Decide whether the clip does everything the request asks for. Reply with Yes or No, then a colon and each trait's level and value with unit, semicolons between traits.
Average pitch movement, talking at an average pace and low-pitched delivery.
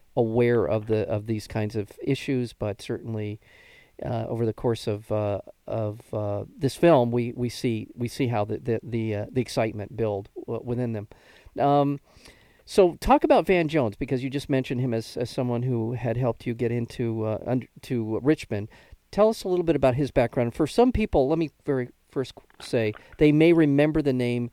Yes: average, 4.2 semitones; average, 195 wpm; low, 120 Hz